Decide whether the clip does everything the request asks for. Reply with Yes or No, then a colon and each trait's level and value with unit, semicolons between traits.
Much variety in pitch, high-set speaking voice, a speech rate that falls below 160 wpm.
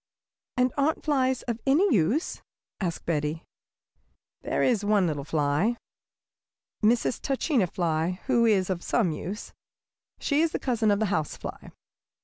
Yes: wide, 7.2 semitones; high, 210 Hz; average, 140 wpm